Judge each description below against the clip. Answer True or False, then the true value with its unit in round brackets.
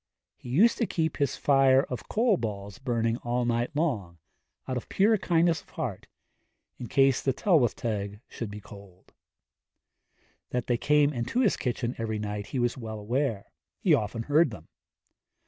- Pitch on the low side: True (125 Hz)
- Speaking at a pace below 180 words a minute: True (165 wpm)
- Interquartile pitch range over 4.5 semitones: True (5.0 semitones)